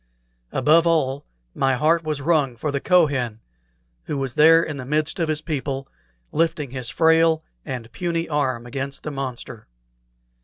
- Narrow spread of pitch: No, average, 3.4 semitones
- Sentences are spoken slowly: No, average, 155 wpm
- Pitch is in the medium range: Yes, medium, 145 Hz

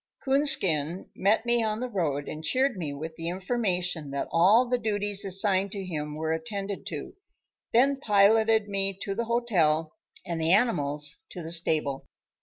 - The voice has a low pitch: No, high, 195 Hz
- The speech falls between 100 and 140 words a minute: No, average, 165 wpm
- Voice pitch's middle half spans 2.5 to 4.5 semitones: No, wide, 5.6 semitones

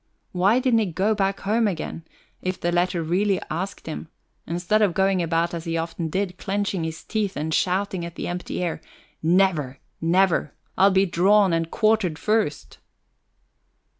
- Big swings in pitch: No, average, 3.1 semitones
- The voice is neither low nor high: Yes, medium, 180 Hz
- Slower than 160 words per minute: No, average, 165 wpm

